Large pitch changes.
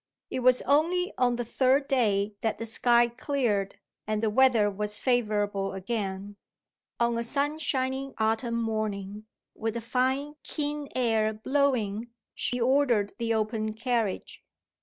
No: average, 3.5 semitones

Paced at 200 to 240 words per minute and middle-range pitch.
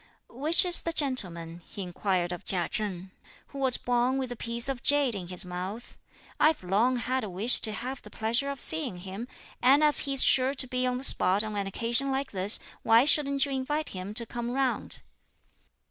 No: fast, 205 wpm; high, 240 Hz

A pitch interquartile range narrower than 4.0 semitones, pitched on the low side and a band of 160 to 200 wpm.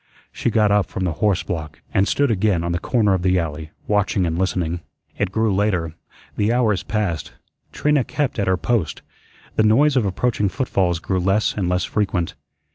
Yes: average, 3.5 semitones; low, 100 Hz; average, 190 wpm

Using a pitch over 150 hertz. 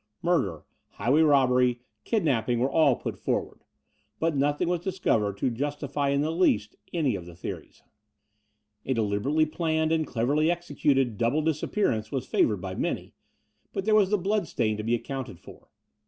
No: medium, 140 Hz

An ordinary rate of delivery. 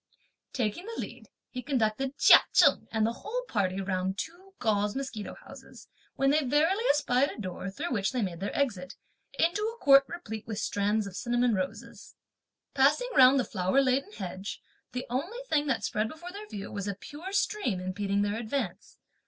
Yes: average, 180 wpm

